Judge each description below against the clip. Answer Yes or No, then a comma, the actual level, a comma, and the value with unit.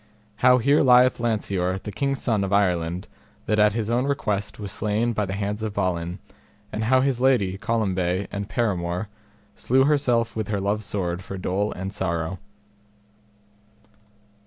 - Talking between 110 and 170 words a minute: Yes, average, 160 wpm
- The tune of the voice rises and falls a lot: No, average, 3.6 semitones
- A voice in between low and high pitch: No, low, 105 Hz